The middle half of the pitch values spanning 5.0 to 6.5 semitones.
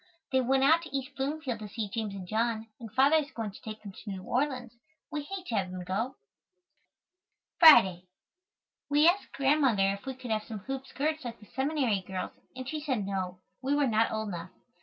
Yes: average, 5.3 semitones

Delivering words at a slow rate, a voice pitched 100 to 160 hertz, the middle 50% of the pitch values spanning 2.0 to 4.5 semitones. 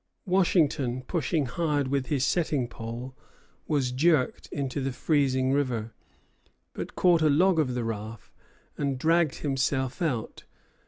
Yes: slow, 130 wpm; low, 135 Hz; average, 3.7 semitones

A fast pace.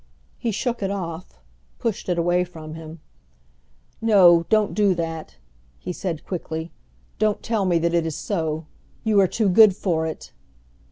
No: average, 160 wpm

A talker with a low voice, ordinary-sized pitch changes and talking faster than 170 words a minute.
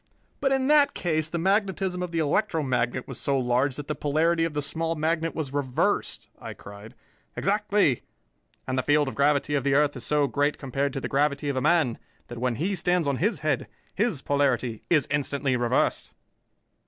No: medium, 145 Hz; average, 3.8 semitones; average, 190 wpm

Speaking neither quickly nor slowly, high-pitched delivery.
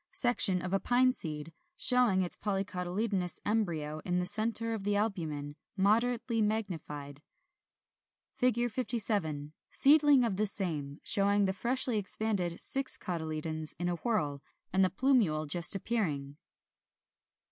No: slow, 125 wpm; high, 195 Hz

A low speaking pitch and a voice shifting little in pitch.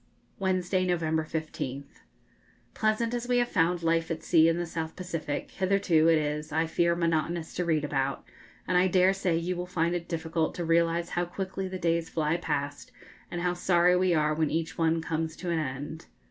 No: medium, 165 Hz; narrow, 2.0 semitones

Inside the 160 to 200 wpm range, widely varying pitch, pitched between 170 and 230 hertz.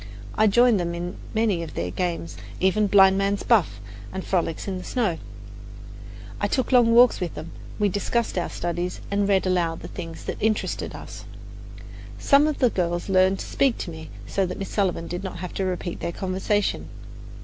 No: average, 190 wpm; average, 3.2 semitones; high, 190 Hz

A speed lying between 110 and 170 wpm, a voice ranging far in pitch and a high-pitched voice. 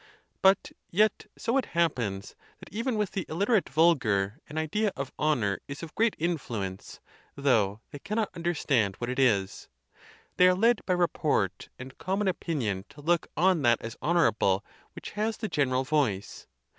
No: average, 165 wpm; wide, 8.2 semitones; medium, 155 Hz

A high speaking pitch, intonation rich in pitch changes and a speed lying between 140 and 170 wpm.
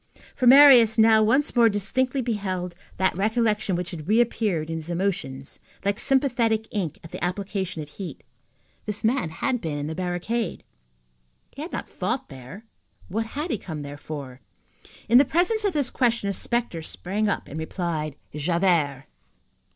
Yes: high, 200 Hz; wide, 6.3 semitones; average, 165 wpm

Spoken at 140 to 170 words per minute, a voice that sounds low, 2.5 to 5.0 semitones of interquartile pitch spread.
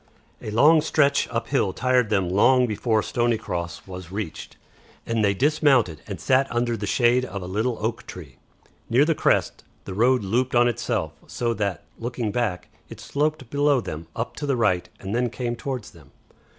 No: average, 185 wpm; low, 115 Hz; average, 4.3 semitones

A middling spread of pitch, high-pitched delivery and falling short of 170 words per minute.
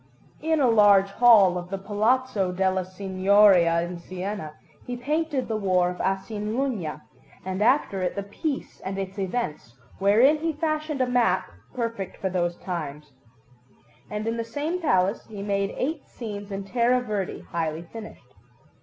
Yes: average, 4.7 semitones; high, 200 Hz; average, 155 wpm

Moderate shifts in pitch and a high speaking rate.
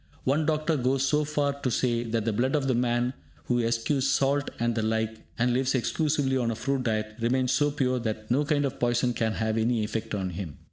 Yes: average, 3.4 semitones; fast, 230 wpm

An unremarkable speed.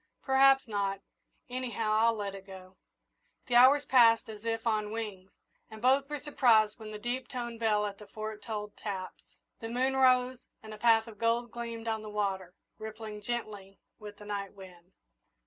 Yes: average, 180 wpm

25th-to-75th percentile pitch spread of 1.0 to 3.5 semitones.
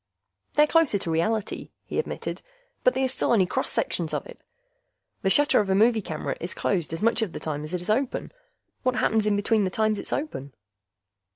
No: wide, 5.5 semitones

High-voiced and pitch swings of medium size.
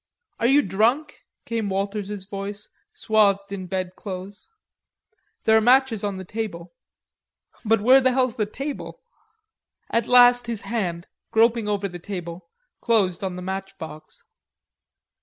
Yes: high, 205 Hz; average, 3.5 semitones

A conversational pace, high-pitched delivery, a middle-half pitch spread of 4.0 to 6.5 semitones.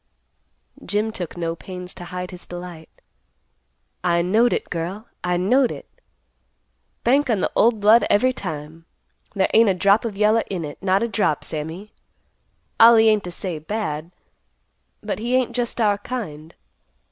Yes: average, 160 wpm; high, 195 Hz; average, 4.3 semitones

